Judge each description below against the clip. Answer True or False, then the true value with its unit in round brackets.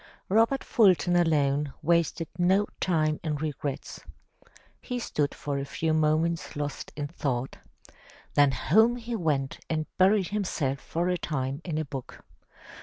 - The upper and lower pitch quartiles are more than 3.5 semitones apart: True (4.0 semitones)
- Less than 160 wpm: True (140 wpm)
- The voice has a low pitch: False (155 Hz)